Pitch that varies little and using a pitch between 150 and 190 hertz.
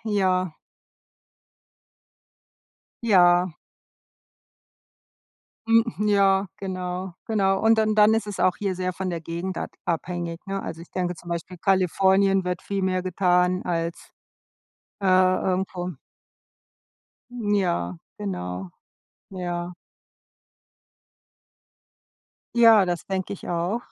Yes: narrow, 2.0 semitones; medium, 185 Hz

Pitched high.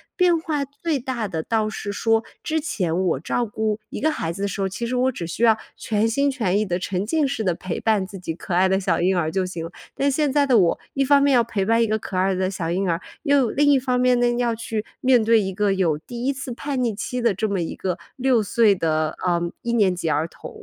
Yes: high, 220 Hz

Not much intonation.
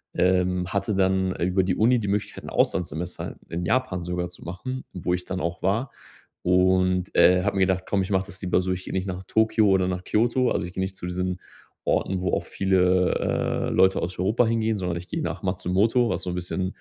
Yes: narrow, 1.6 semitones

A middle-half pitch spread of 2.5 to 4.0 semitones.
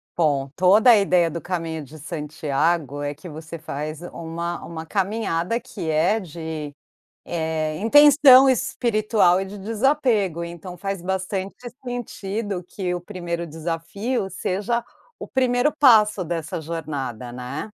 No: average, 4.8 semitones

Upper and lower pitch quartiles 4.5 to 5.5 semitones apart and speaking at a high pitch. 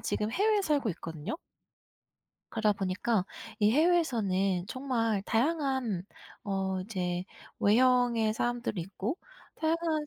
No: wide, 5.9 semitones; high, 225 Hz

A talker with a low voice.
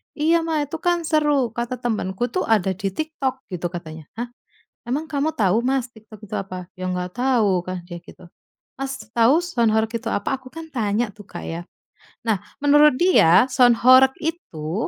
No: high, 235 Hz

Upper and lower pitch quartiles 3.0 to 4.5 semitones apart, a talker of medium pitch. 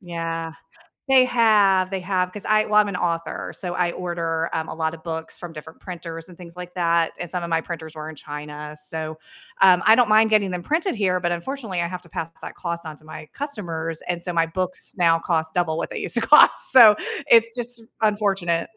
Yes: average, 3.7 semitones; medium, 175 Hz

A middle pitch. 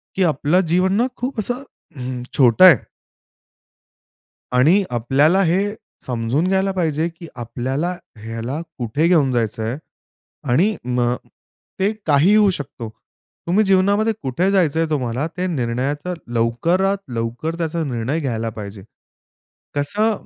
Yes: medium, 150 Hz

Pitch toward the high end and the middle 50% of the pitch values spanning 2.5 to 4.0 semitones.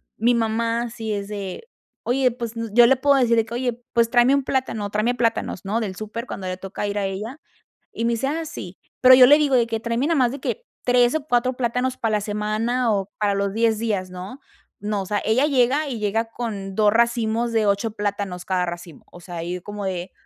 Yes: high, 225 Hz; average, 3.3 semitones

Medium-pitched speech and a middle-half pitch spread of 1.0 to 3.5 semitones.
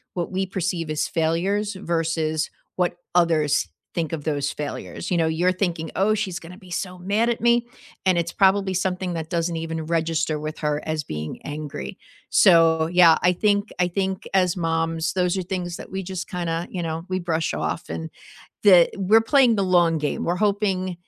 Yes: medium, 175 Hz; average, 2.7 semitones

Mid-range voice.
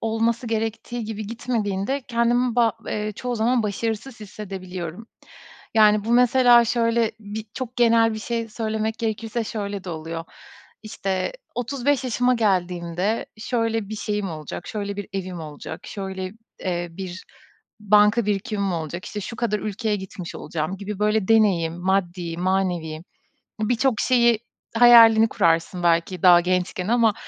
No: high, 210 Hz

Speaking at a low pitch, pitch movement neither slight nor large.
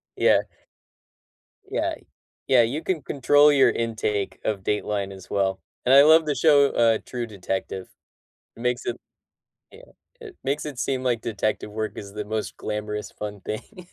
Yes: low, 115 Hz; average, 5.0 semitones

